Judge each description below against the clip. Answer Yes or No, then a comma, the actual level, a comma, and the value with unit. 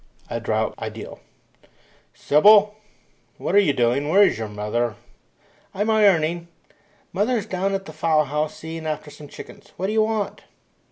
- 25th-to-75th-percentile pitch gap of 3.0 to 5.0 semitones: No, wide, 5.5 semitones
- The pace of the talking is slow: No, average, 155 wpm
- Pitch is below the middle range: No, medium, 165 Hz